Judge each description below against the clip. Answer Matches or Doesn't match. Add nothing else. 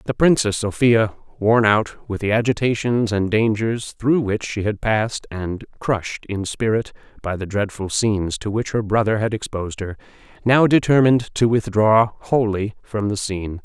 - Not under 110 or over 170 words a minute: Matches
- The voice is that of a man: Matches